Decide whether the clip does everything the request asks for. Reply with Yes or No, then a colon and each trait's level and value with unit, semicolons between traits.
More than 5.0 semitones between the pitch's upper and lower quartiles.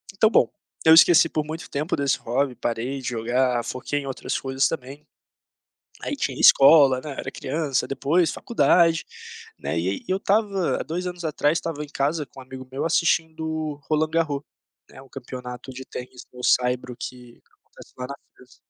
No: average, 4.0 semitones